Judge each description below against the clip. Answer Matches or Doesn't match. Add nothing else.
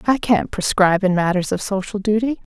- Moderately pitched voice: Doesn't match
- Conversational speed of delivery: Matches